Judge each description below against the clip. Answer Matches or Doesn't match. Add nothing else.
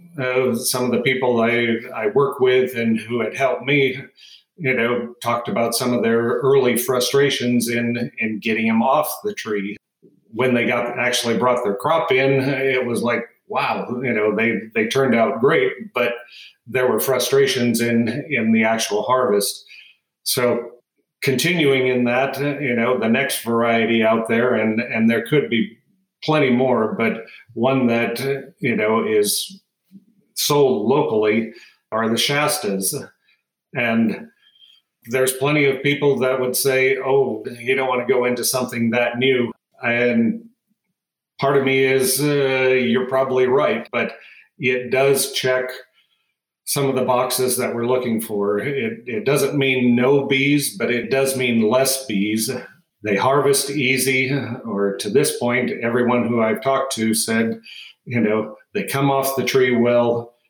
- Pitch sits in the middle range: Doesn't match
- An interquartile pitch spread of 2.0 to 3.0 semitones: Matches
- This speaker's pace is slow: Doesn't match